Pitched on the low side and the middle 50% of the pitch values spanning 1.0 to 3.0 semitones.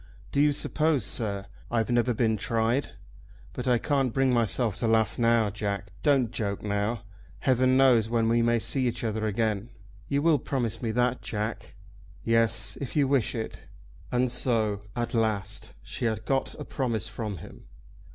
Yes: low, 115 Hz; average, 2.7 semitones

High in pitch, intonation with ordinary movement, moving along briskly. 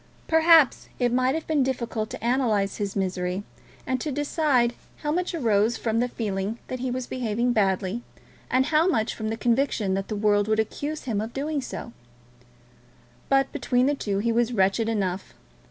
No: high, 235 Hz; average, 4.2 semitones; average, 180 wpm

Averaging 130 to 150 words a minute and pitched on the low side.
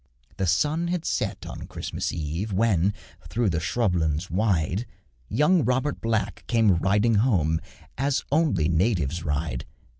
Yes: average, 140 wpm; low, 100 Hz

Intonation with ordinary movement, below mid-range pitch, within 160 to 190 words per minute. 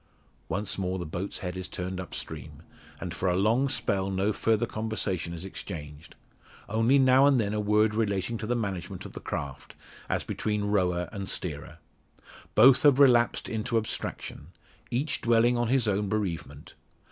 Yes: average, 4.0 semitones; low, 105 Hz; average, 165 wpm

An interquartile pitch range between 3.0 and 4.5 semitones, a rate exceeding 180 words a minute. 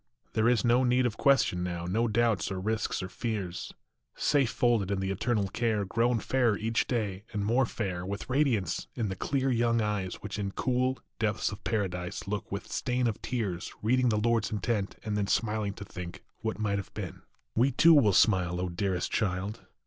Yes: average, 3.5 semitones; average, 195 wpm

